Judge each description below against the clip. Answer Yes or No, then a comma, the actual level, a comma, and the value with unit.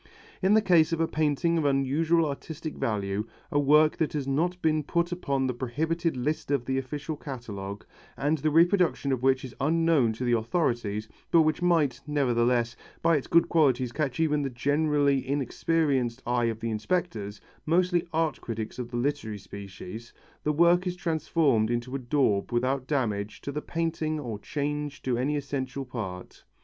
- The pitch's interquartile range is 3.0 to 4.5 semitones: No, average, 4.9 semitones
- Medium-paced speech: Yes, average, 175 wpm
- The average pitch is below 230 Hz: Yes, medium, 140 Hz